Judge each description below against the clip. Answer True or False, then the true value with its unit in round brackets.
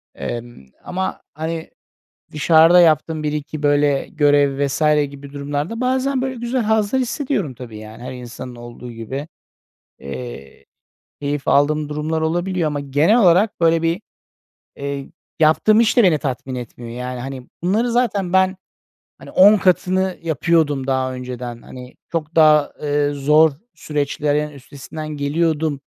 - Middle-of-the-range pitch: True (150 Hz)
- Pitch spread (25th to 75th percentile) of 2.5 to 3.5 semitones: False (4.2 semitones)